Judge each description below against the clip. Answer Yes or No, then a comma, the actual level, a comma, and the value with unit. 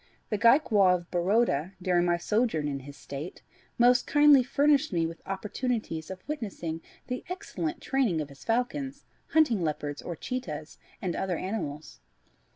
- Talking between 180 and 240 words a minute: No, average, 150 wpm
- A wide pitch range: Yes, wide, 7.4 semitones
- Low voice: No, high, 190 Hz